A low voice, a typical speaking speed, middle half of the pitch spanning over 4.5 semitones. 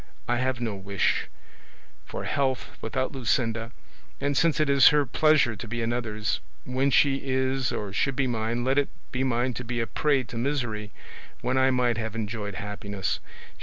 No: low, 120 Hz; average, 175 wpm; average, 3.0 semitones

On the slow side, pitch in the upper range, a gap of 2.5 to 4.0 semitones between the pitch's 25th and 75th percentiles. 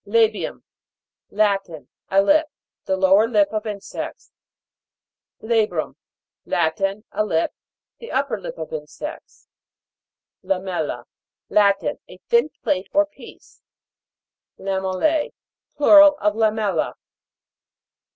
Yes: slow, 100 wpm; high, 210 Hz; average, 3.6 semitones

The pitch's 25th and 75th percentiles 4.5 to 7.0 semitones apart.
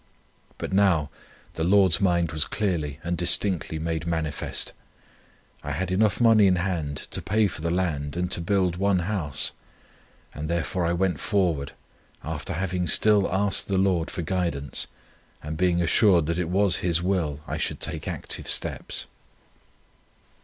No: average, 3.0 semitones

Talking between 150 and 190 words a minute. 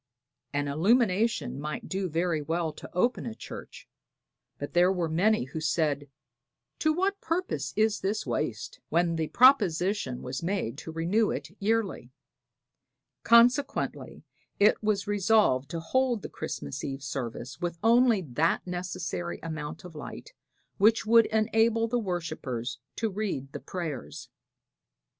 No: slow, 135 wpm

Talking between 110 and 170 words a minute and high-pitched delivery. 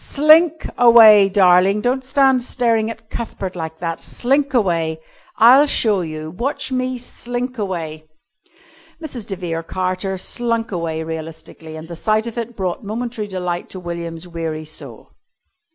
Yes: average, 145 wpm; high, 200 Hz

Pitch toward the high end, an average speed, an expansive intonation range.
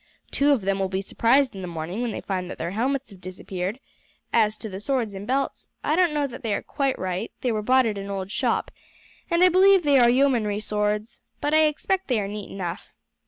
No: high, 220 Hz; fast, 235 wpm; wide, 5.9 semitones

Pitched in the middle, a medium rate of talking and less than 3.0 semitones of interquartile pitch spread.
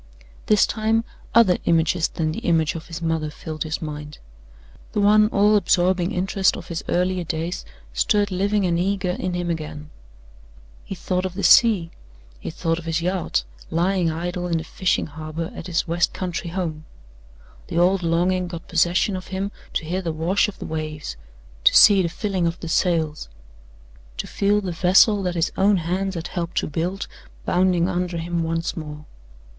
Yes: medium, 175 Hz; average, 180 wpm; narrow, 2.5 semitones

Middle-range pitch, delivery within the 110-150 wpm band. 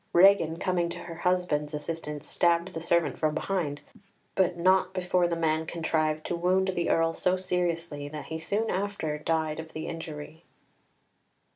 No: medium, 170 Hz; average, 160 wpm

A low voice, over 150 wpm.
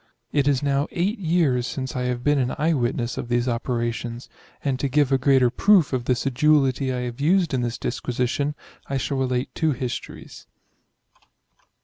Yes: low, 130 Hz; average, 185 wpm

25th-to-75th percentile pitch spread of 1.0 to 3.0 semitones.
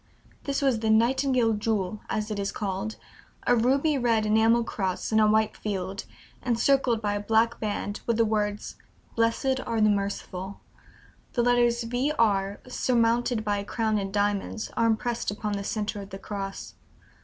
Yes: narrow, 2.5 semitones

